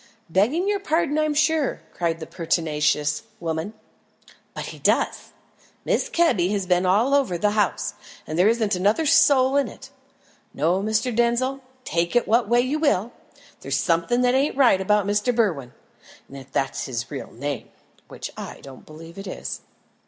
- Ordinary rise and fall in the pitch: No, wide, 7.5 semitones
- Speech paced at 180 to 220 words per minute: No, average, 165 wpm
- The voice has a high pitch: Yes, high, 210 Hz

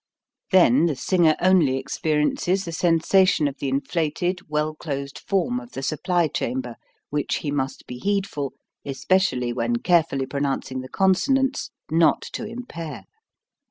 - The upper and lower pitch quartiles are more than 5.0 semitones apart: Yes, wide, 5.4 semitones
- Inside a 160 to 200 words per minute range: No, slow, 135 wpm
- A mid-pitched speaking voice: Yes, medium, 155 Hz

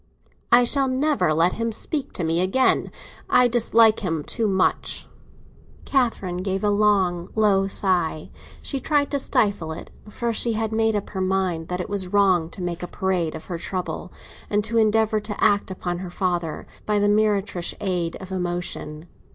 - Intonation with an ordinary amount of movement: Yes, average, 3.7 semitones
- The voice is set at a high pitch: Yes, high, 195 Hz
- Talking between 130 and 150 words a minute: No, average, 175 wpm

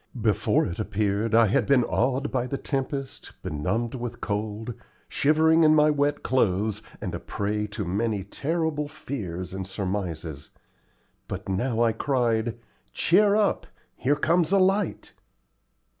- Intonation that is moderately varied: No, wide, 6.1 semitones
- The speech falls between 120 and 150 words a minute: Yes, average, 140 wpm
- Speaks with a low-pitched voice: Yes, low, 115 Hz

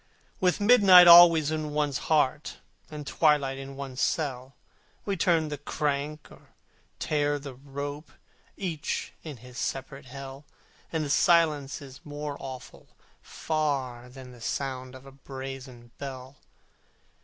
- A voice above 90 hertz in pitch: Yes, medium, 140 Hz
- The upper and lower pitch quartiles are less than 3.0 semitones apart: Yes, narrow, 2.5 semitones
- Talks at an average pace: No, slow, 130 wpm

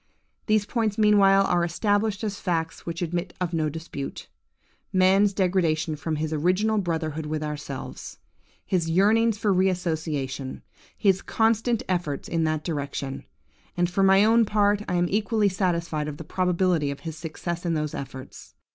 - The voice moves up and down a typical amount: Yes, average, 4.1 semitones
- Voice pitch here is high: No, medium, 175 Hz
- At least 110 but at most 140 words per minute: No, average, 155 wpm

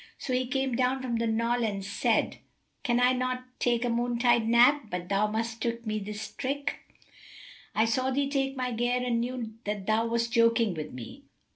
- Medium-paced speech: Yes, average, 190 wpm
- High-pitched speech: Yes, high, 235 Hz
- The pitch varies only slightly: Yes, narrow, 2.3 semitones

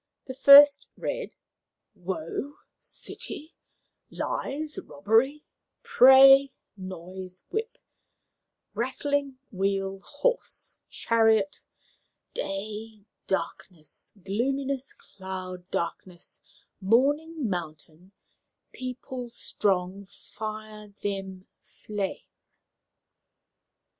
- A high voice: Yes, high, 215 Hz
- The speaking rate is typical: No, slow, 65 wpm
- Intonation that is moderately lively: No, wide, 6.2 semitones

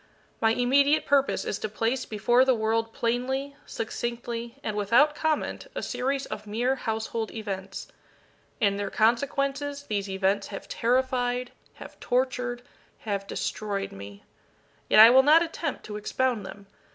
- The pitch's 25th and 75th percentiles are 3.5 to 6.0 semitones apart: Yes, average, 3.8 semitones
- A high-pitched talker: Yes, high, 235 Hz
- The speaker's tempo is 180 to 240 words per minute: No, average, 140 wpm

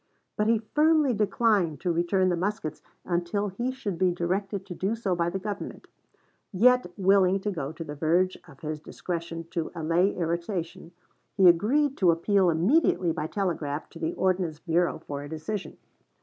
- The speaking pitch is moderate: Yes, medium, 180 Hz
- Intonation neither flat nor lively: Yes, average, 3.6 semitones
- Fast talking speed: No, average, 170 wpm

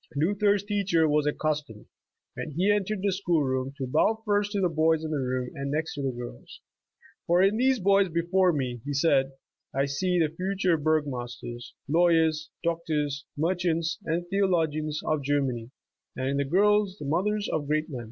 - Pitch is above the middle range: No, medium, 160 Hz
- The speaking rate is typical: Yes, average, 180 wpm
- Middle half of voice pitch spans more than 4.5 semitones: Yes, average, 4.9 semitones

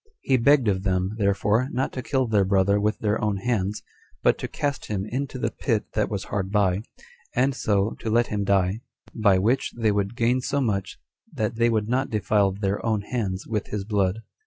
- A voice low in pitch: Yes, low, 105 Hz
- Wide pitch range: No, average, 3.1 semitones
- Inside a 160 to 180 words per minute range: No, fast, 205 wpm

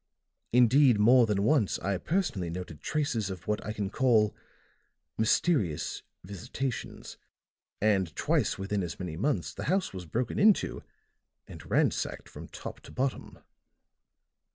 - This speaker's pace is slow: Yes, slow, 130 wpm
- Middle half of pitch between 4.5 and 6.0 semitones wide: Yes, wide, 5.5 semitones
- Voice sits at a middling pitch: No, low, 105 Hz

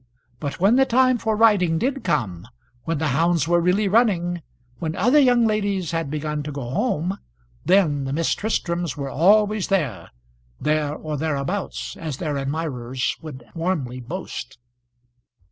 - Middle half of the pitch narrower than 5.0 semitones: No, wide, 5.6 semitones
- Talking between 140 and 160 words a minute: Yes, average, 150 wpm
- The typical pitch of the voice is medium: Yes, medium, 165 Hz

